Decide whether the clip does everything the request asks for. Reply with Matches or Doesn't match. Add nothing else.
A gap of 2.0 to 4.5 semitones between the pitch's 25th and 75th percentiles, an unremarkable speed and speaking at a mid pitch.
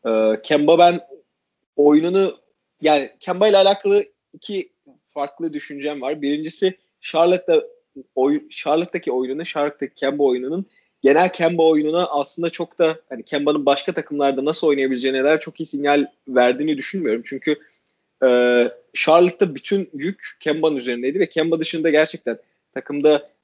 Matches